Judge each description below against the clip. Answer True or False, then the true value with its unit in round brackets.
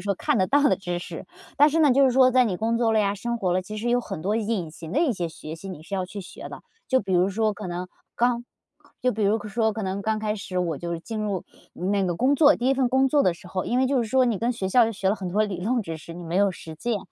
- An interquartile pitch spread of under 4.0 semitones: False (4.7 semitones)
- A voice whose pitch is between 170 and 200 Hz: False (210 Hz)